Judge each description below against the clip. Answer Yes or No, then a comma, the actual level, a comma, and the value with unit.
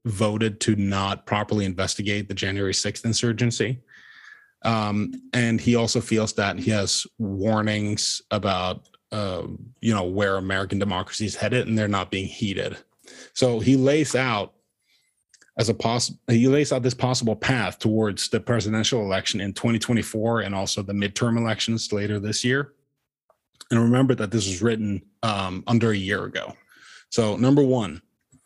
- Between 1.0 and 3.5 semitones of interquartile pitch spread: Yes, average, 3.0 semitones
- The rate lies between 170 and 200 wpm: No, average, 160 wpm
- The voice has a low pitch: Yes, low, 110 Hz